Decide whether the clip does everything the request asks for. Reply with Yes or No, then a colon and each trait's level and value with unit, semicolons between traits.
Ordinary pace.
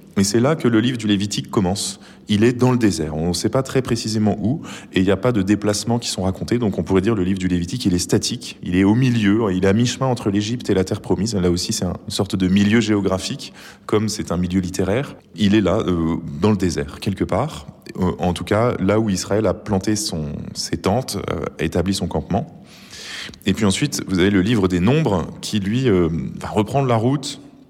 No: fast, 240 wpm